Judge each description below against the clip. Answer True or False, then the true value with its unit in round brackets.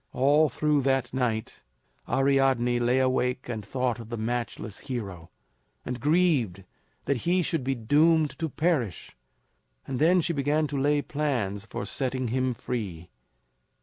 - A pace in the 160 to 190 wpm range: False (145 wpm)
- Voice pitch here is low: True (130 Hz)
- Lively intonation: False (3.7 semitones)